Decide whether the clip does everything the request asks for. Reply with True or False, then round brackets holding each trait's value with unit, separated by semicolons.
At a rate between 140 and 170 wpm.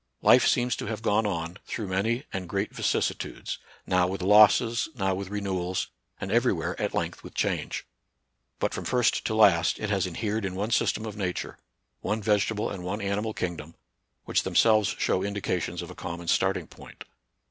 False (180 wpm)